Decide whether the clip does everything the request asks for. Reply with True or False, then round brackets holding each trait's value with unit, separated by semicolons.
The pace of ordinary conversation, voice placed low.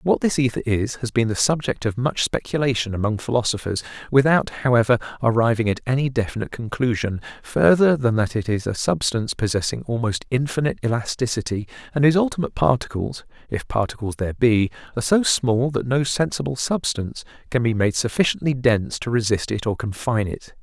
True (165 wpm; 120 Hz)